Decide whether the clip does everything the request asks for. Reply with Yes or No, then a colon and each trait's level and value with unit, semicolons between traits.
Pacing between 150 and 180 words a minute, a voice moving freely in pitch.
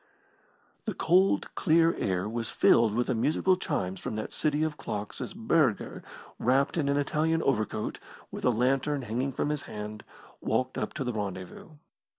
Yes: average, 165 wpm; wide, 6.0 semitones